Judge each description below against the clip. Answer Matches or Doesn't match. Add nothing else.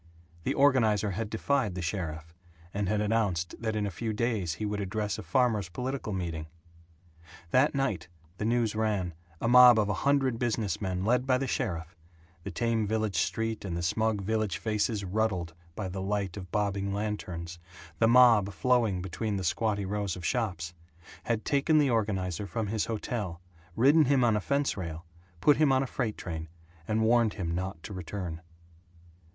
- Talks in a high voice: Doesn't match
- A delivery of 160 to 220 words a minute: Matches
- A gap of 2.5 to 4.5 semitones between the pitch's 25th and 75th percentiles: Matches